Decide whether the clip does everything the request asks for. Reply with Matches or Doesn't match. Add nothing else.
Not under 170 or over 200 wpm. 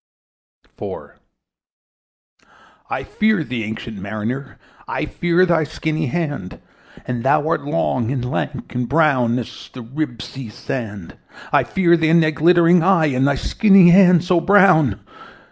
Doesn't match